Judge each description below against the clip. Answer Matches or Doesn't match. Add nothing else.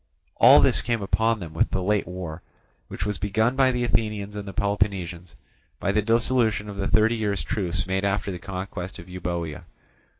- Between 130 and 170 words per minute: Doesn't match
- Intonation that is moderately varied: Matches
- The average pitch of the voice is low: Matches